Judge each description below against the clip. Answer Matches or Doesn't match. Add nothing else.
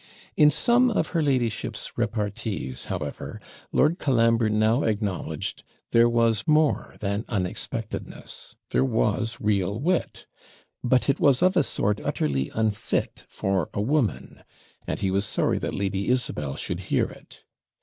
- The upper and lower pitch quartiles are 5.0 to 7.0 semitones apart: Matches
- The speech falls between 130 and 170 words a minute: Matches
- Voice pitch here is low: Matches